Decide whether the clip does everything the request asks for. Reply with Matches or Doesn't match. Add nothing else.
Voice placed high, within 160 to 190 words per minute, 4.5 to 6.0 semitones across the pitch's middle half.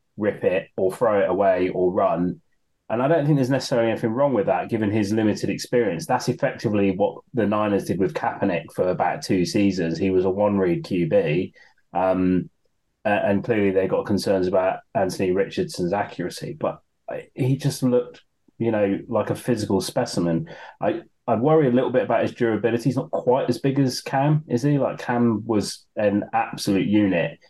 Doesn't match